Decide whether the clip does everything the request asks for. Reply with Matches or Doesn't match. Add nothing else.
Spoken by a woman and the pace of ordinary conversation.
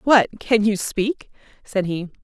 Matches